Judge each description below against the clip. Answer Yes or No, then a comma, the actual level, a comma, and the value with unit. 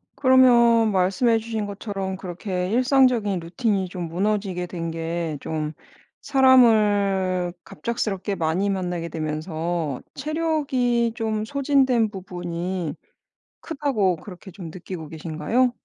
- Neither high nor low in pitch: No, high, 195 Hz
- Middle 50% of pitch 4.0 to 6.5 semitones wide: Yes, average, 5.2 semitones